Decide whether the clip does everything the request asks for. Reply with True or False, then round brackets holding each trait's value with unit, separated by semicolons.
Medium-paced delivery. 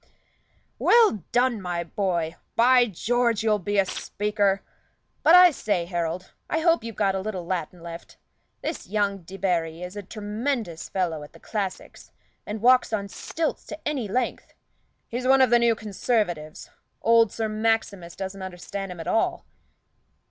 True (155 wpm)